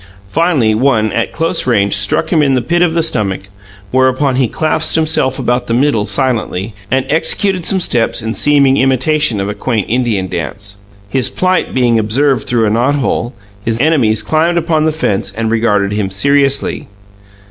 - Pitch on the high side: No, low, 130 Hz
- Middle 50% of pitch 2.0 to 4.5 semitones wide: No, average, 5.3 semitones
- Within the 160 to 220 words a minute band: Yes, average, 170 wpm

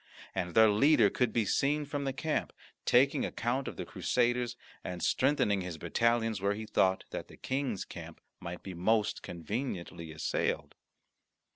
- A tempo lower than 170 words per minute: Yes, average, 155 wpm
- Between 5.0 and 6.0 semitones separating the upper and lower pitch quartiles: Yes, wide, 5.5 semitones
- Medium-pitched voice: No, low, 110 Hz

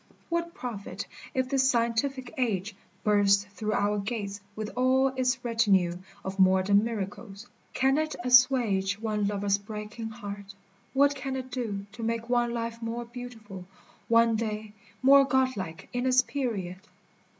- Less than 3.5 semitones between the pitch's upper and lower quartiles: No, average, 4.0 semitones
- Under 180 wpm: Yes, average, 140 wpm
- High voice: Yes, high, 230 Hz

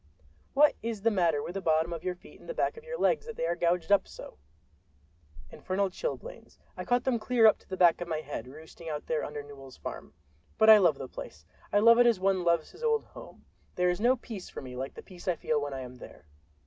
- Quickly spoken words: Yes, fast, 250 wpm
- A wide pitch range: Yes, wide, 6.6 semitones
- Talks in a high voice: No, medium, 180 Hz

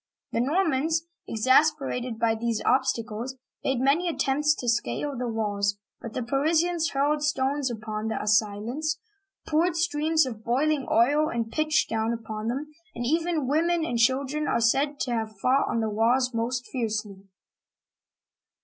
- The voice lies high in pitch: Yes, very high, 260 Hz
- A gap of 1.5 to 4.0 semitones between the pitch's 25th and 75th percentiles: No, average, 4.9 semitones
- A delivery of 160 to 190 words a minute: No, average, 150 wpm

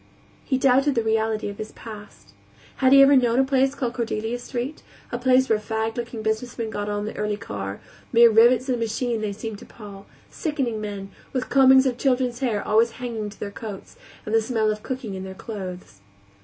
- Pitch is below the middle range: No, high, 225 Hz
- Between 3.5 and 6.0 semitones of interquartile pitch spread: No, average, 3.1 semitones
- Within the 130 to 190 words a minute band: No, fast, 205 wpm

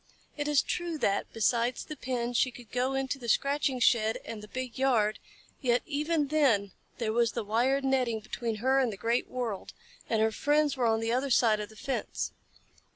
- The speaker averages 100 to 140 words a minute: No, average, 200 wpm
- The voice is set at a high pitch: Yes, high, 245 Hz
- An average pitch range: Yes, average, 3.2 semitones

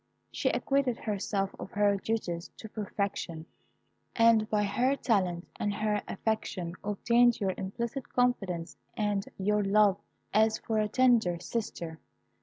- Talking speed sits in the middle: No, slow, 130 wpm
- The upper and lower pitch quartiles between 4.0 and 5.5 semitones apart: No, average, 2.7 semitones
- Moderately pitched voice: No, high, 210 Hz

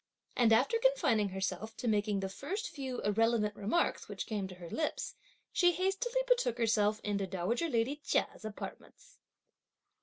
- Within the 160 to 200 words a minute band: No, average, 150 wpm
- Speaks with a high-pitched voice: Yes, high, 230 Hz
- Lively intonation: Yes, wide, 8.5 semitones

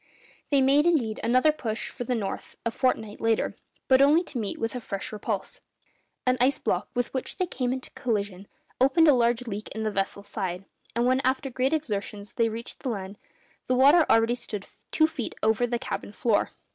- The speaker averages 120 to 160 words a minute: No, average, 195 wpm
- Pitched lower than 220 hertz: No, high, 240 Hz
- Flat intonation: No, average, 3.5 semitones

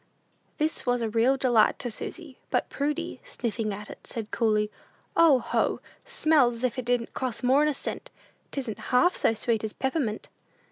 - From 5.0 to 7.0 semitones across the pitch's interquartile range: No, average, 3.9 semitones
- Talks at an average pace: Yes, average, 180 wpm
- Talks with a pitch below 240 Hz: No, high, 245 Hz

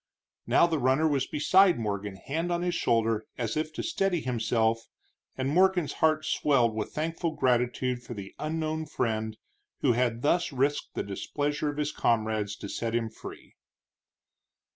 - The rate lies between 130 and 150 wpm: No, average, 160 wpm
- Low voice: Yes, low, 130 Hz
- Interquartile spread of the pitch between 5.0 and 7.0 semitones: Yes, wide, 5.5 semitones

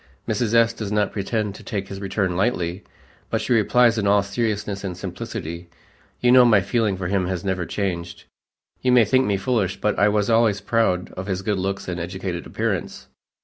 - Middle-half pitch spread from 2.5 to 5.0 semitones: Yes, average, 3.1 semitones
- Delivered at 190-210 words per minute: Yes, average, 195 wpm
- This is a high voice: No, low, 100 Hz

